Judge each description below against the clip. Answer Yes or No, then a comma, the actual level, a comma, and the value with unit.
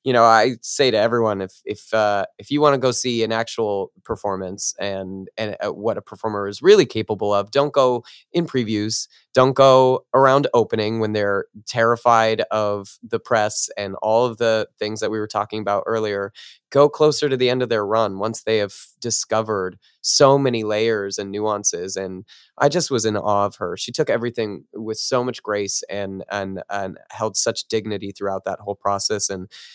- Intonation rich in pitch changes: No, average, 3.0 semitones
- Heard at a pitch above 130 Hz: No, low, 110 Hz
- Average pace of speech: Yes, average, 195 wpm